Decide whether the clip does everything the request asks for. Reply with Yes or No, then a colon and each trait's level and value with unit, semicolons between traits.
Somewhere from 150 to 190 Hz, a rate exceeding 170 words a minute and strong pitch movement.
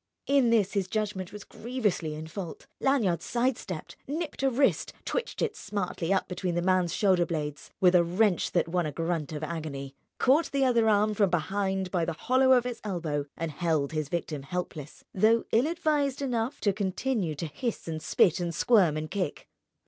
Yes: medium, 185 Hz; average, 185 wpm; wide, 6.0 semitones